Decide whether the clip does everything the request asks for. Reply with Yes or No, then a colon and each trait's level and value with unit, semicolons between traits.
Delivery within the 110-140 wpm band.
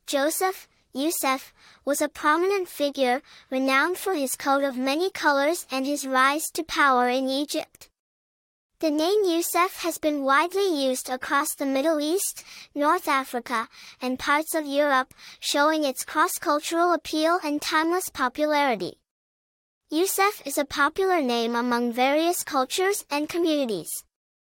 Yes: slow, 135 wpm